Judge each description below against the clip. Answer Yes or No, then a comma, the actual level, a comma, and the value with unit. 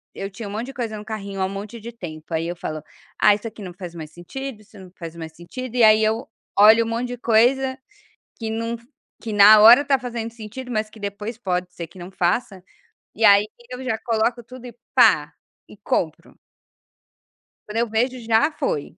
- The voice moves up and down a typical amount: Yes, average, 3.4 semitones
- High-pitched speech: Yes, high, 220 Hz